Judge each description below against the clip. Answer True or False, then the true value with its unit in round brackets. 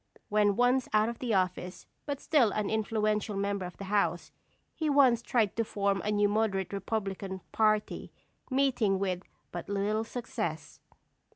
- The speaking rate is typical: True (150 wpm)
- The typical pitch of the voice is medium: False (210 Hz)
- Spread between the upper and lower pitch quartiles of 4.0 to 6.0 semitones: False (2.5 semitones)